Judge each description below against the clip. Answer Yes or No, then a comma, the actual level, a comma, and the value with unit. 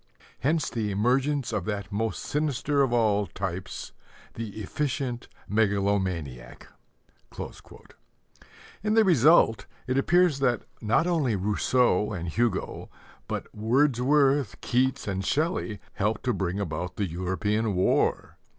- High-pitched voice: No, low, 115 Hz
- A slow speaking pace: Yes, slow, 115 wpm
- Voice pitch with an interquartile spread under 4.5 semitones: No, wide, 5.4 semitones